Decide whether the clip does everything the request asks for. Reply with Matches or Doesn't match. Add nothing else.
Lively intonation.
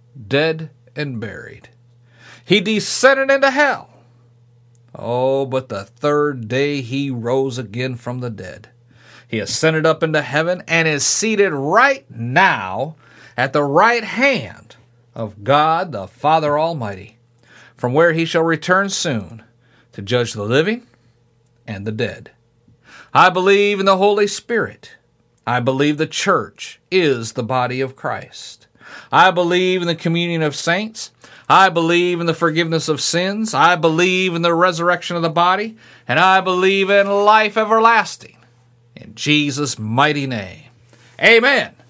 Matches